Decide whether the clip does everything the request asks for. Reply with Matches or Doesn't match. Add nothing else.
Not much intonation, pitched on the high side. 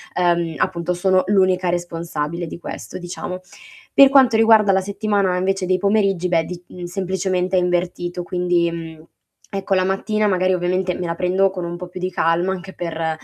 Doesn't match